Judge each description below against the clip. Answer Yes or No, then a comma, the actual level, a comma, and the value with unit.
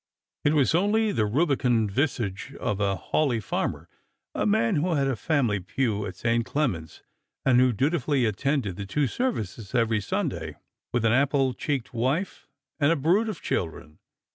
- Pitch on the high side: No, low, 125 Hz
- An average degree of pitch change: No, wide, 5.7 semitones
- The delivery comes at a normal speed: Yes, average, 165 wpm